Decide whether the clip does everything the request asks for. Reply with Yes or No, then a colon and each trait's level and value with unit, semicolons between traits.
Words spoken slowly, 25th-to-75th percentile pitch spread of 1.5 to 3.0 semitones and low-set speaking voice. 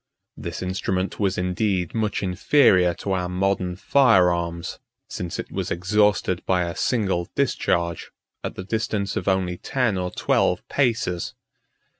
No: average, 145 wpm; narrow, 2.4 semitones; very low, 95 Hz